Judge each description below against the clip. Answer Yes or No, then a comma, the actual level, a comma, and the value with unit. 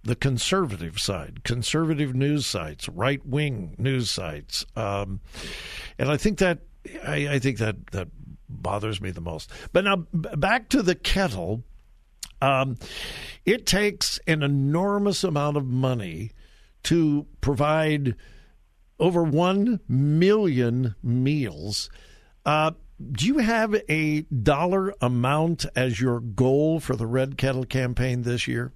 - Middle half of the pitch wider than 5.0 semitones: Yes, wide, 5.5 semitones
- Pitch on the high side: No, low, 135 Hz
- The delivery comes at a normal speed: No, slow, 130 wpm